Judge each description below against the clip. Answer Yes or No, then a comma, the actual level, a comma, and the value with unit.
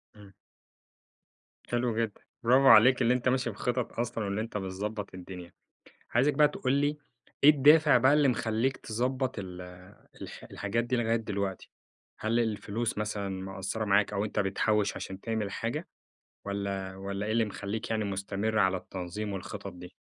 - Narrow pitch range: No, average, 3.4 semitones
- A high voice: No, low, 110 Hz